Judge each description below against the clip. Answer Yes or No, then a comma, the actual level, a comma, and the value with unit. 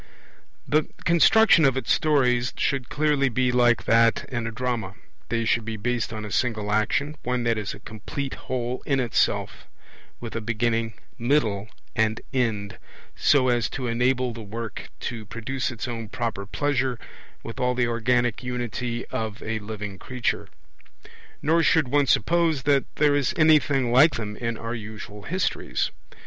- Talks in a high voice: No, low, 120 Hz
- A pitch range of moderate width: Yes, average, 3.1 semitones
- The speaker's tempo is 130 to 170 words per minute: Yes, average, 160 wpm